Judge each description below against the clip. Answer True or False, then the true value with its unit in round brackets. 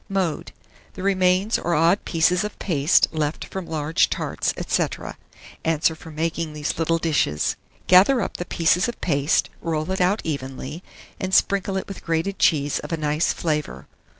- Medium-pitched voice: True (165 Hz)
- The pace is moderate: True (165 wpm)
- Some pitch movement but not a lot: True (3.4 semitones)